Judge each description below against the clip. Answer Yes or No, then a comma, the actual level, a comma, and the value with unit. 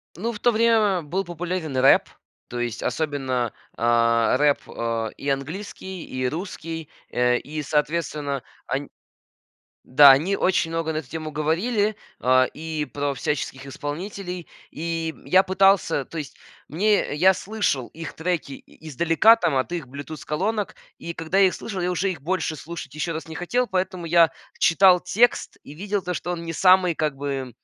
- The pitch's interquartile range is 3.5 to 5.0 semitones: Yes, average, 4.6 semitones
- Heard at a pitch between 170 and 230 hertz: No, medium, 160 Hz